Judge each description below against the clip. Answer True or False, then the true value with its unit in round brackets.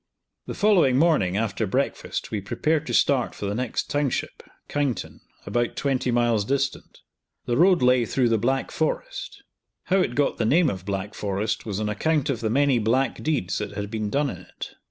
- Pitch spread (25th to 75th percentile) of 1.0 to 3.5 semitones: False (5.1 semitones)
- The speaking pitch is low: True (125 Hz)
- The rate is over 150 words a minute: True (190 wpm)